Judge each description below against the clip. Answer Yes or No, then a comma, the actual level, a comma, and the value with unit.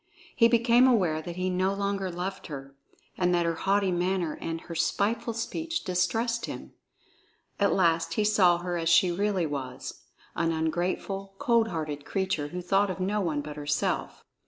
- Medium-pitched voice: Yes, medium, 180 Hz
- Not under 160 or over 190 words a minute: Yes, average, 170 wpm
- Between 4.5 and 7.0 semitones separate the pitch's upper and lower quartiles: No, average, 3.4 semitones